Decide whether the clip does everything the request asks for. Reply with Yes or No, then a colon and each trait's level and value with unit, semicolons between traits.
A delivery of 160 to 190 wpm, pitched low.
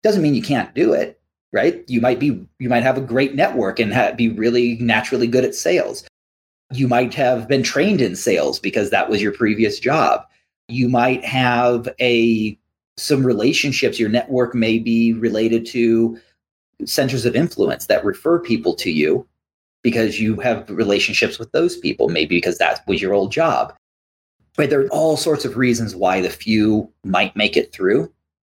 Yes: average, 180 wpm; low, 120 Hz